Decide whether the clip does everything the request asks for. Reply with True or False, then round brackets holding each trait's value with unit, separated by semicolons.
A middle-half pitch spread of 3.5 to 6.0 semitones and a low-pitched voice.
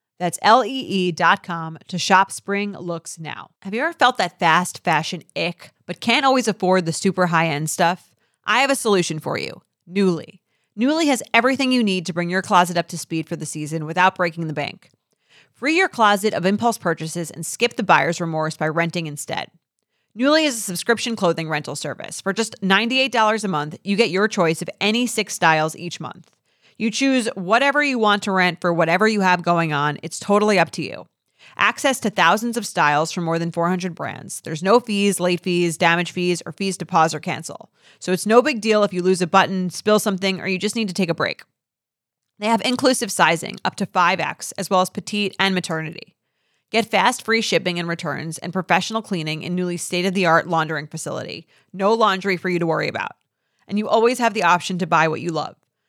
False (4.2 semitones; 180 Hz)